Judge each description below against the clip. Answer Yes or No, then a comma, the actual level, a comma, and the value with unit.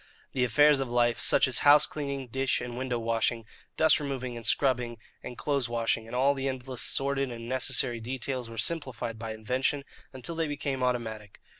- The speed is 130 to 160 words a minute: No, average, 180 wpm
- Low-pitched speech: Yes, low, 130 Hz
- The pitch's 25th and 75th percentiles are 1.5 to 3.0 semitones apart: Yes, average, 2.7 semitones